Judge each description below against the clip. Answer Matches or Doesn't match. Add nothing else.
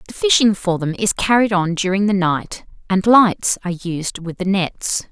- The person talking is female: Matches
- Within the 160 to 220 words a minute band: Matches